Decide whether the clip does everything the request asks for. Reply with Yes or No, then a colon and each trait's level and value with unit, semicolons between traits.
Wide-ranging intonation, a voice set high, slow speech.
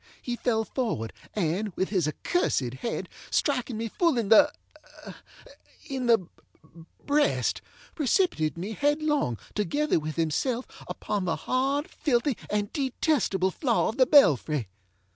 Yes: wide, 7.3 semitones; high, 235 Hz; slow, 125 wpm